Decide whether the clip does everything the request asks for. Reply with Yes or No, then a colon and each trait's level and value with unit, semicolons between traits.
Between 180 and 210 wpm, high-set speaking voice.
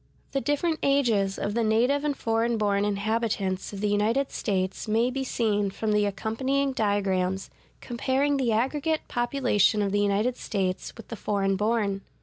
No: average, 160 wpm; high, 220 Hz